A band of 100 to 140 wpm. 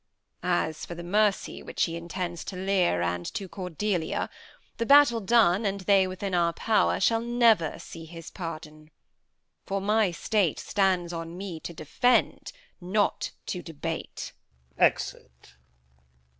Yes: slow, 135 wpm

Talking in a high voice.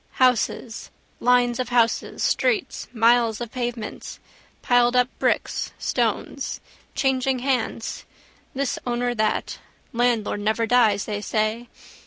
Yes: high, 240 Hz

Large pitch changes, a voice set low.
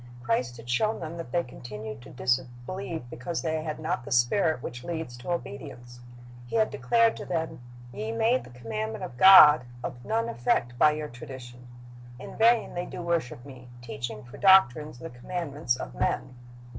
Yes: wide, 5.8 semitones; low, 130 Hz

